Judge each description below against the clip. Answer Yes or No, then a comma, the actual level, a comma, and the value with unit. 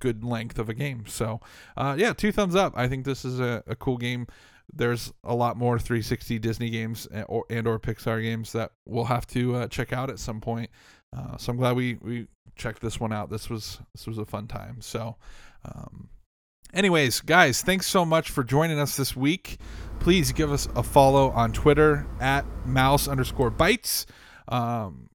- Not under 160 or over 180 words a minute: No, average, 200 wpm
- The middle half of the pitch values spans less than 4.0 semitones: Yes, average, 3.2 semitones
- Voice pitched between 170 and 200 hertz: No, low, 120 Hz